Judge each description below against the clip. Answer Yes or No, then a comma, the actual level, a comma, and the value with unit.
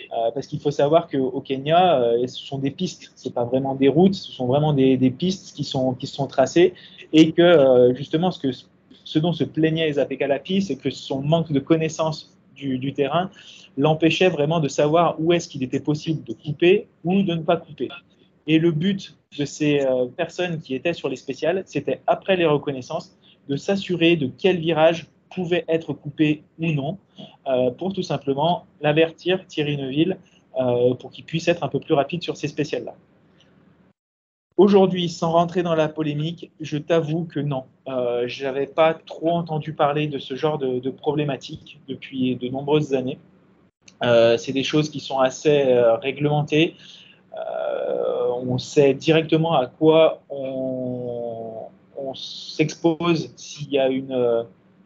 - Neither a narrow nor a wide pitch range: Yes, average, 4.0 semitones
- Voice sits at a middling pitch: Yes, medium, 150 Hz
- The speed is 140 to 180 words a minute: Yes, average, 175 wpm